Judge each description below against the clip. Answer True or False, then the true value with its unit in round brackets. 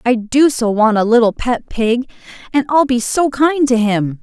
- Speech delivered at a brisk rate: True (215 wpm)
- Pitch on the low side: False (245 Hz)